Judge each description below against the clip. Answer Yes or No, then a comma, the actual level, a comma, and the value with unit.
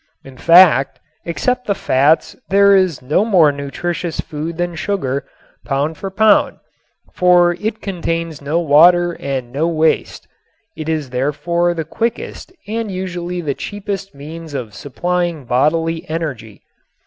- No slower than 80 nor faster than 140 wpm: Yes, slow, 135 wpm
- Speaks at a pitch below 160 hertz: No, medium, 165 Hz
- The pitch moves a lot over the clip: No, average, 3.7 semitones